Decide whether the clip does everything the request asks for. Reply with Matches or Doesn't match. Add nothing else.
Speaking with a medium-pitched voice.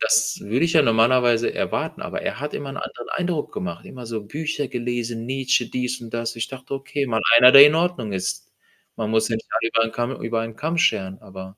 Doesn't match